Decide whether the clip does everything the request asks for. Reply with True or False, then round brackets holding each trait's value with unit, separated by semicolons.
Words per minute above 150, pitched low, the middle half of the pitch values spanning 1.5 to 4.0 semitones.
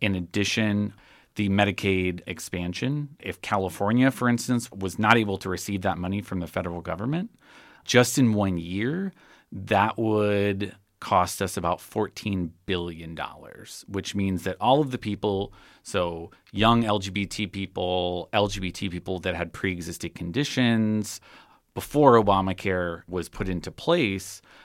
False (135 wpm; 100 Hz; 3.0 semitones)